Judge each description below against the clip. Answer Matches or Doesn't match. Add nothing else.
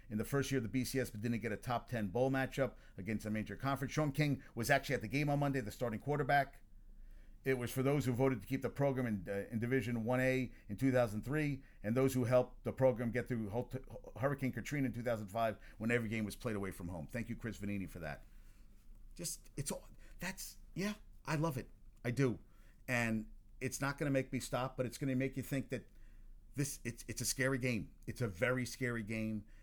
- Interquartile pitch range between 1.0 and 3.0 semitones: Doesn't match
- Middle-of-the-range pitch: Doesn't match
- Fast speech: Matches